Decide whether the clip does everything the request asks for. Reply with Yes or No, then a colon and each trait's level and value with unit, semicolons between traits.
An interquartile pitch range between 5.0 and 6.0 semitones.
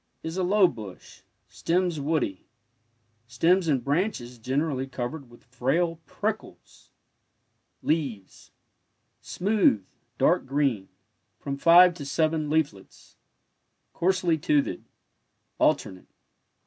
Yes: average, 5.3 semitones